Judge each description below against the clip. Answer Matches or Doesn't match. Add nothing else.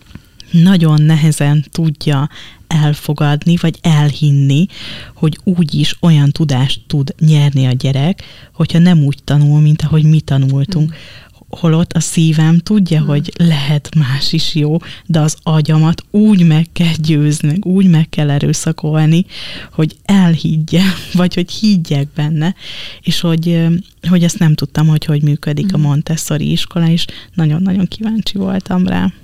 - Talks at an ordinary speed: Matches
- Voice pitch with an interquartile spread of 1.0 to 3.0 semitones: Matches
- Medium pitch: Matches